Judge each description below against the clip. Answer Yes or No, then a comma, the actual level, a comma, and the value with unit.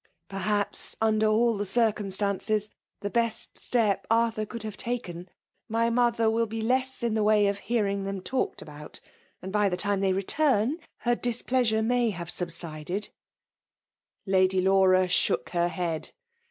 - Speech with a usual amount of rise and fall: Yes, average, 3.4 semitones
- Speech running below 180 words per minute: Yes, average, 155 wpm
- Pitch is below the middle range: No, high, 210 Hz